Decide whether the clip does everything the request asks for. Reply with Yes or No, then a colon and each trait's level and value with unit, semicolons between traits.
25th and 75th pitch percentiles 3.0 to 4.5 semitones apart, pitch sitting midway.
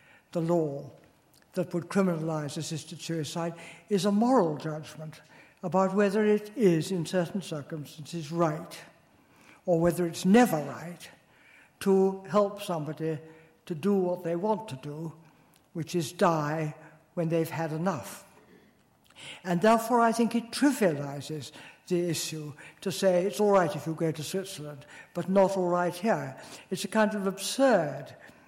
Yes: average, 3.6 semitones; medium, 170 Hz